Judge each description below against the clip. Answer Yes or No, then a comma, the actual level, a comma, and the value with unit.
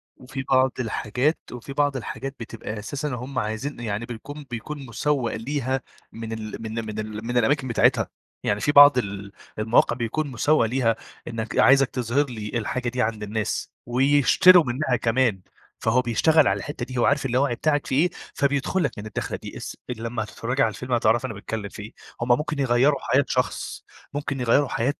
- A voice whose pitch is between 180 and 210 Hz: No, low, 125 Hz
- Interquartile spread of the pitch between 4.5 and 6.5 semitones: No, average, 3.6 semitones